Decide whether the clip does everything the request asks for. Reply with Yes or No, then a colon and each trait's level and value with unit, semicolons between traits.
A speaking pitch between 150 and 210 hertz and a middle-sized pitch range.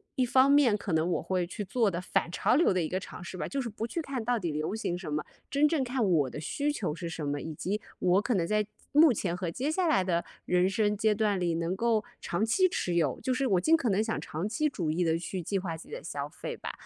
No: high, 195 Hz; wide, 6.3 semitones